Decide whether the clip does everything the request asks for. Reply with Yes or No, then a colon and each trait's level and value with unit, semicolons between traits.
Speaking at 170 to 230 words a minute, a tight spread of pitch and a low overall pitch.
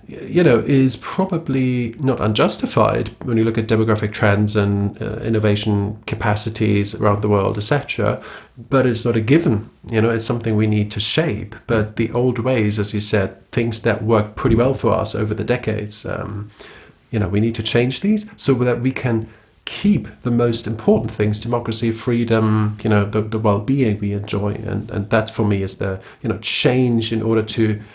Yes: average, 190 wpm; narrow, 2.2 semitones; low, 110 Hz